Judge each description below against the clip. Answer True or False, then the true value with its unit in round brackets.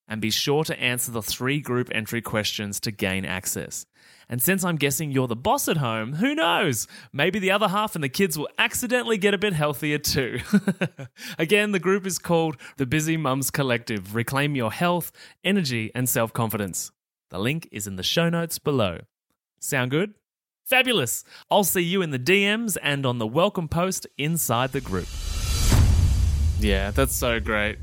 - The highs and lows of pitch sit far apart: True (8.3 semitones)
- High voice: False (140 Hz)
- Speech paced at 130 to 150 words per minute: False (180 wpm)